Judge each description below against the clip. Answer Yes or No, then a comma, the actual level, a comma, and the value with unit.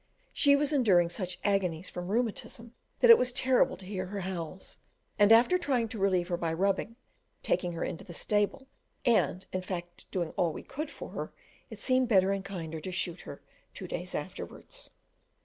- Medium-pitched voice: No, high, 195 Hz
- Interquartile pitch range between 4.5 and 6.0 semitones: Yes, average, 5.1 semitones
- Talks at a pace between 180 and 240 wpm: Yes, average, 185 wpm